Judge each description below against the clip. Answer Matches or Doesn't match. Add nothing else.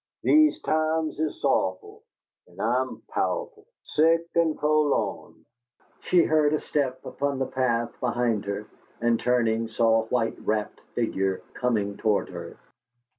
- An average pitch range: Doesn't match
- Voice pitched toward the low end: Matches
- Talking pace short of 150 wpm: Matches